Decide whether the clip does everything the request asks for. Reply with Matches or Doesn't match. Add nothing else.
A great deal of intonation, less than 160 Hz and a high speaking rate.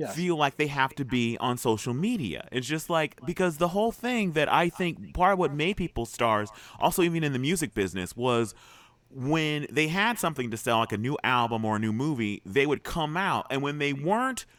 Matches